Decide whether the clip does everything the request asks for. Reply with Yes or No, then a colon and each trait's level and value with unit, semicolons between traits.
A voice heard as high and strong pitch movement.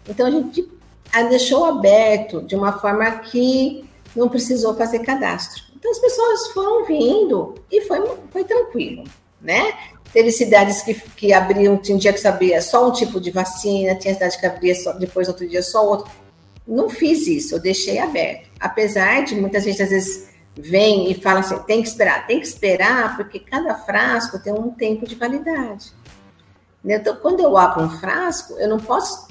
Yes: high, 220 Hz; wide, 6.3 semitones